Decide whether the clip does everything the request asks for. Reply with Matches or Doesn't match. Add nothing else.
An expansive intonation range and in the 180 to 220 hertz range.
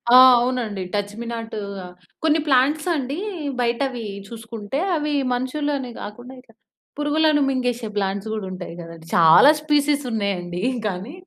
Doesn't match